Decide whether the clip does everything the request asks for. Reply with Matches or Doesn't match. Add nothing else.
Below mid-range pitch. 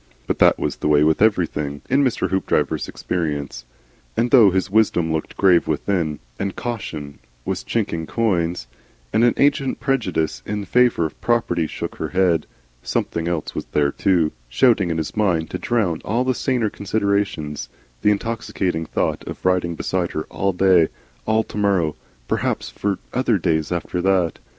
Matches